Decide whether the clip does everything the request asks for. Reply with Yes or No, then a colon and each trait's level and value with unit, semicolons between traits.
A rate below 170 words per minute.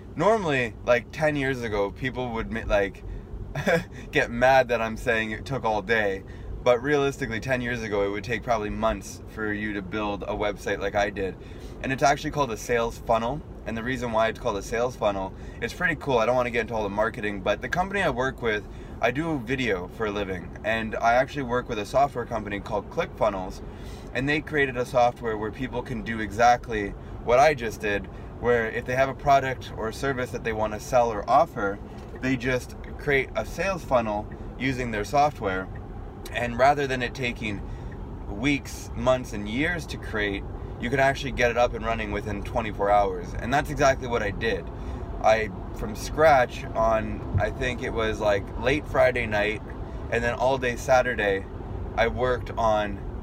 No: average, 195 wpm